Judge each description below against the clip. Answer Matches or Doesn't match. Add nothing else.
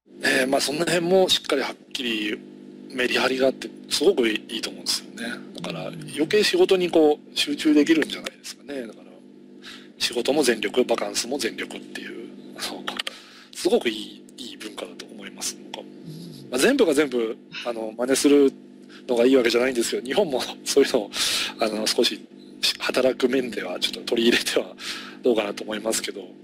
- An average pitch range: Doesn't match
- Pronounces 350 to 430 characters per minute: Matches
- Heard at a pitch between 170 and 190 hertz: Doesn't match